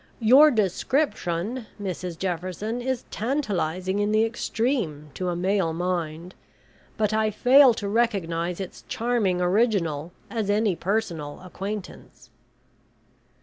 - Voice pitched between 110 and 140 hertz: No, high, 200 Hz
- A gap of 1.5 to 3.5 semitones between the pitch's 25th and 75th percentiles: No, average, 4.3 semitones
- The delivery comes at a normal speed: No, slow, 110 wpm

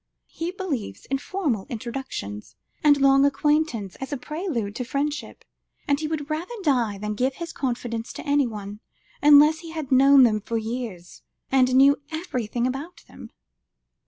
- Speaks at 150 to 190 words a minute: Yes, average, 155 wpm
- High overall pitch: Yes, very high, 270 Hz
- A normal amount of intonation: Yes, average, 4.6 semitones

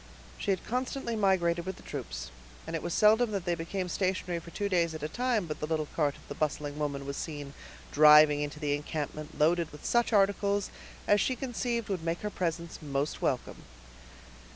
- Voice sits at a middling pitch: Yes, medium, 170 Hz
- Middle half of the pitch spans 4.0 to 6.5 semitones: Yes, average, 4.9 semitones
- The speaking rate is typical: Yes, average, 195 wpm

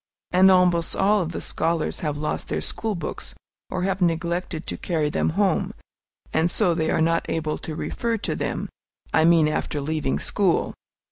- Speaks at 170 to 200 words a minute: Yes, average, 180 wpm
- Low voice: No, medium, 170 Hz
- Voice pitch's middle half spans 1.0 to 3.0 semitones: Yes, narrow, 2.6 semitones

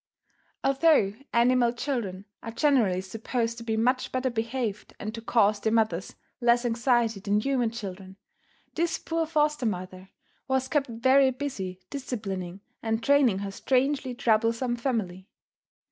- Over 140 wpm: No, slow, 135 wpm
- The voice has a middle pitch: No, high, 230 Hz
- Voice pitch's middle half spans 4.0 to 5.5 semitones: Yes, average, 4.3 semitones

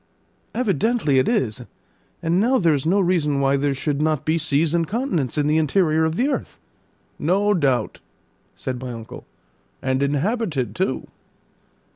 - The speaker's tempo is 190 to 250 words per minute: No, average, 155 wpm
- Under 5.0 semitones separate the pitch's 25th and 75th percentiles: No, wide, 5.4 semitones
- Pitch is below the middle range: No, medium, 155 Hz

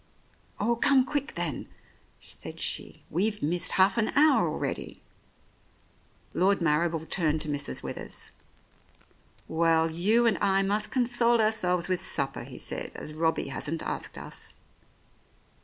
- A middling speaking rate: No, slow, 130 wpm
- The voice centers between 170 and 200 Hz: Yes, medium, 185 Hz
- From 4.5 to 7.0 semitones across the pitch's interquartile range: Yes, wide, 5.4 semitones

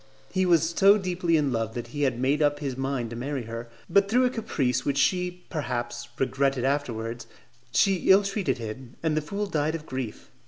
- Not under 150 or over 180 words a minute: No, average, 200 wpm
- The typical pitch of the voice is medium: Yes, medium, 145 Hz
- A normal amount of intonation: No, wide, 6.4 semitones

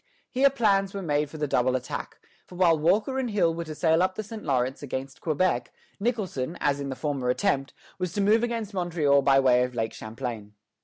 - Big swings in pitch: Yes, wide, 6.5 semitones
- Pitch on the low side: No, medium, 160 Hz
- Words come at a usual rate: No, fast, 210 wpm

